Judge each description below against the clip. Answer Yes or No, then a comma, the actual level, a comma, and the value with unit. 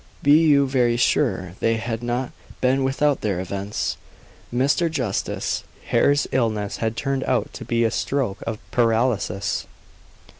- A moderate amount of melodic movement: Yes, average, 3.5 semitones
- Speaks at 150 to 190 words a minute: No, average, 140 wpm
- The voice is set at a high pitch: No, low, 120 Hz